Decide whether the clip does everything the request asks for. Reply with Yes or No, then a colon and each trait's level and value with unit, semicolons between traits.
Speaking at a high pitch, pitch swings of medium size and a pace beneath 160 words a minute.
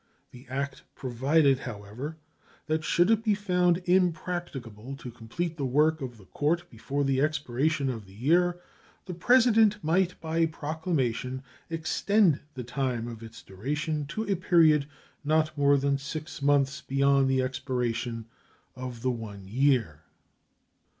No: medium, 140 Hz; average, 4.5 semitones; average, 140 wpm